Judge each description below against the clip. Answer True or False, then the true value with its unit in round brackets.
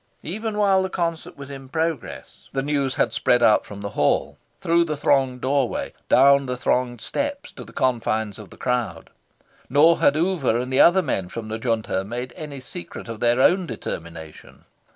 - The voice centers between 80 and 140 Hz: True (135 Hz)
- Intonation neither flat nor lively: False (5.8 semitones)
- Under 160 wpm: False (185 wpm)